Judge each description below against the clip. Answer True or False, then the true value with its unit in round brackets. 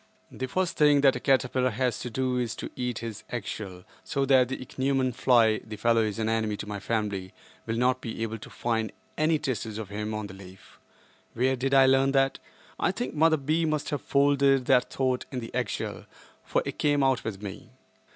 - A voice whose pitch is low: True (125 Hz)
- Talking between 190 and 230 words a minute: True (200 wpm)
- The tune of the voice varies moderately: True (3.5 semitones)